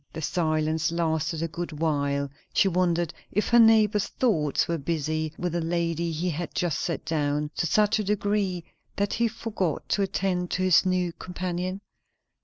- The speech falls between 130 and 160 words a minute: No, average, 170 wpm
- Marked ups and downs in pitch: No, average, 3.1 semitones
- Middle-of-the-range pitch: Yes, medium, 175 Hz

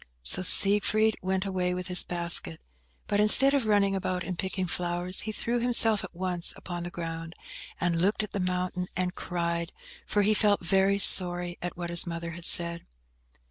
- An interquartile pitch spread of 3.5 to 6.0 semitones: No, narrow, 2.5 semitones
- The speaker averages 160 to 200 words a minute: Yes, average, 180 wpm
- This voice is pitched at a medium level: Yes, medium, 180 Hz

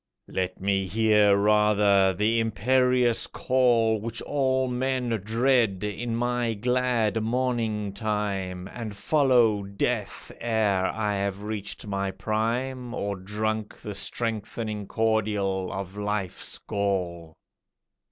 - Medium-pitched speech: No, low, 110 Hz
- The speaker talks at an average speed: No, slow, 110 wpm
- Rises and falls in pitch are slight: No, average, 3.0 semitones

